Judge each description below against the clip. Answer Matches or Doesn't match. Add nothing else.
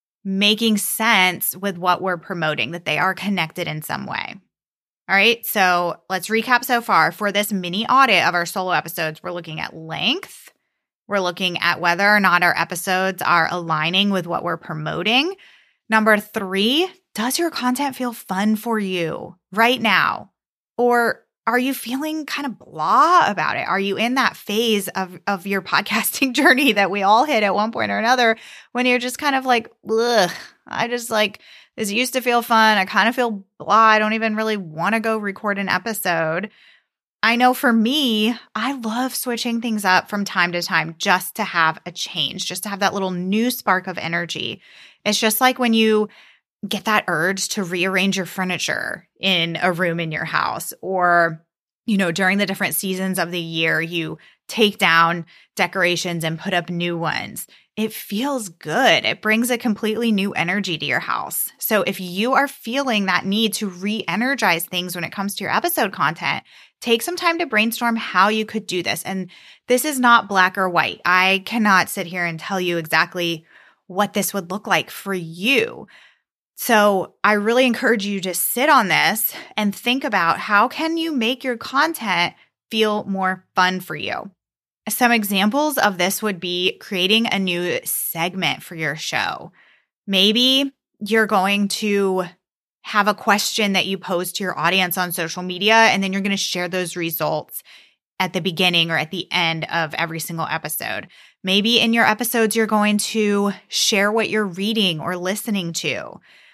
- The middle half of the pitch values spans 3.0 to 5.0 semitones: Matches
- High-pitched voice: Matches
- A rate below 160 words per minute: Doesn't match